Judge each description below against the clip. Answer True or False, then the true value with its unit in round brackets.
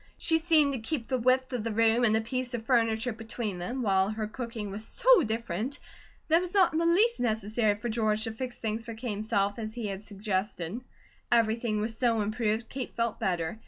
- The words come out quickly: True (215 wpm)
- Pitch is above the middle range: True (225 Hz)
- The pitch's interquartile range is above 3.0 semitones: False (2.7 semitones)